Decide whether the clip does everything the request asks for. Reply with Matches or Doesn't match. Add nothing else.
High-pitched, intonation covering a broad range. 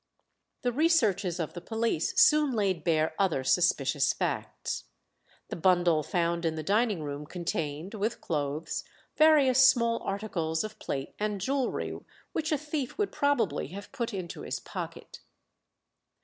Matches